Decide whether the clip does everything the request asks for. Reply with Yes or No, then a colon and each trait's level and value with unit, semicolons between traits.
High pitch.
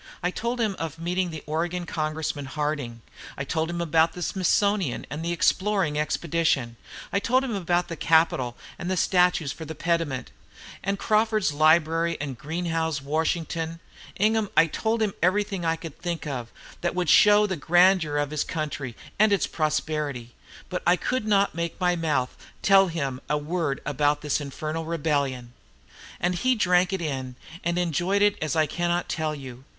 No: medium, 165 Hz